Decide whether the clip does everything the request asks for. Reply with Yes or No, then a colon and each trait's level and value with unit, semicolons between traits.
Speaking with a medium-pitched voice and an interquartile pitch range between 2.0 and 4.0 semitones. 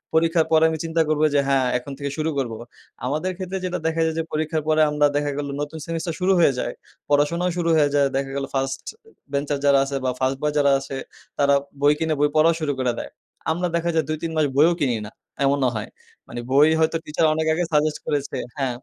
Yes: medium, 150 Hz; narrow, 2.5 semitones